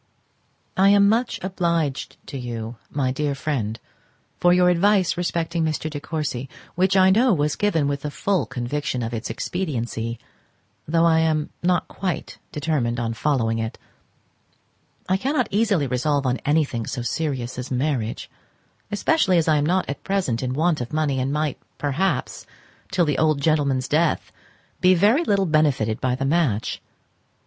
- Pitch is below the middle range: No, medium, 150 Hz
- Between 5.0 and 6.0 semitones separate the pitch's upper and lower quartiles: Yes, wide, 5.6 semitones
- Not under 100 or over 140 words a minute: No, average, 160 wpm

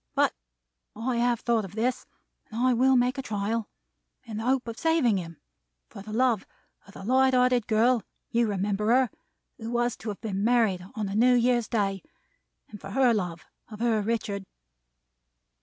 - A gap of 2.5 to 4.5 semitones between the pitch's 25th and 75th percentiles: Yes, average, 2.9 semitones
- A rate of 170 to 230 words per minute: Yes, average, 180 wpm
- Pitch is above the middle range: Yes, high, 230 Hz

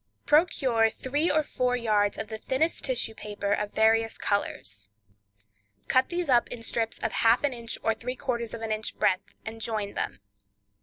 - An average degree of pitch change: Yes, average, 3.0 semitones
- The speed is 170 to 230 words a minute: Yes, average, 175 wpm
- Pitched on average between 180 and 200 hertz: No, high, 225 Hz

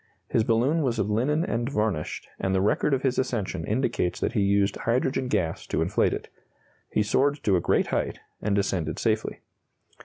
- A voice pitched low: Yes, low, 110 Hz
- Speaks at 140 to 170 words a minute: No, average, 185 wpm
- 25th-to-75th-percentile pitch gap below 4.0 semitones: No, average, 4.6 semitones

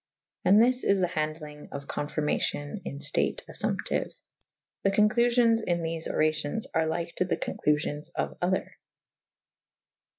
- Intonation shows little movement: No, average, 5.1 semitones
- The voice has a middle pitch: Yes, medium, 165 Hz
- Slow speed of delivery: Yes, slow, 130 wpm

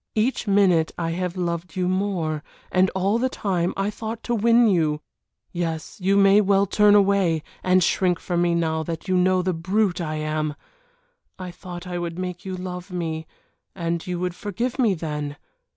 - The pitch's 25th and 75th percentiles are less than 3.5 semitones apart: Yes, average, 2.8 semitones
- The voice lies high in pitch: No, medium, 180 Hz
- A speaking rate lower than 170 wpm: No, average, 185 wpm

